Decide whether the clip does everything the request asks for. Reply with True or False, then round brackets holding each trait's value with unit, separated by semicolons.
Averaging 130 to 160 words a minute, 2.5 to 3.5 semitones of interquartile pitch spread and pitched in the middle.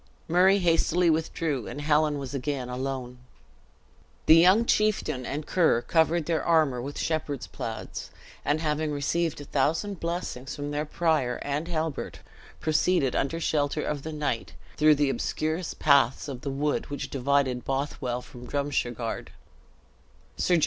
True (140 wpm; 3.1 semitones; 150 Hz)